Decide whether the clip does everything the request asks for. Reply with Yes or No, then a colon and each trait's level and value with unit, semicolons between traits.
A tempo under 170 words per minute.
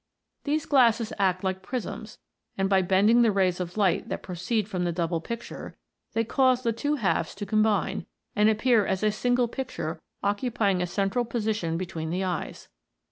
No: average, 175 wpm